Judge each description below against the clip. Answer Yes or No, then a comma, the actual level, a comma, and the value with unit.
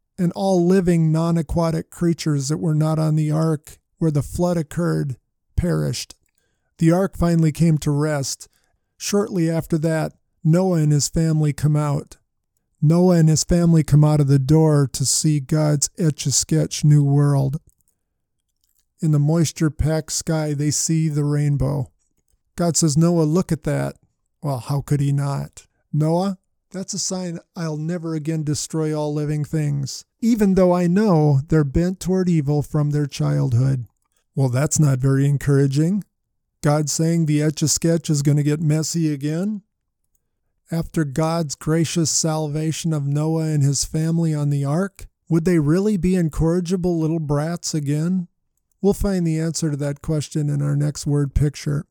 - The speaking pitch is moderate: Yes, medium, 155 Hz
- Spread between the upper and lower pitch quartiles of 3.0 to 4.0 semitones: No, narrow, 2.4 semitones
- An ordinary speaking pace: Yes, average, 160 wpm